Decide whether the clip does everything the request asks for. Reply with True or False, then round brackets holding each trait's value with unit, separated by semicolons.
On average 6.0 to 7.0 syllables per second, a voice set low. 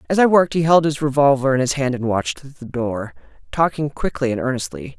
False (5.8 syllables/s; 130 Hz)